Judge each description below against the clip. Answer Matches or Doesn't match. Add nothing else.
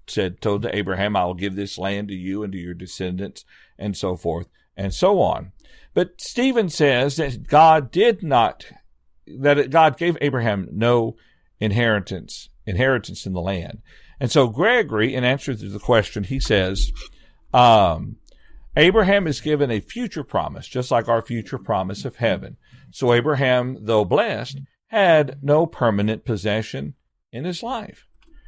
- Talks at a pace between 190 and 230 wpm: Doesn't match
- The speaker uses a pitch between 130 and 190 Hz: Doesn't match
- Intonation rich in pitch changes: Matches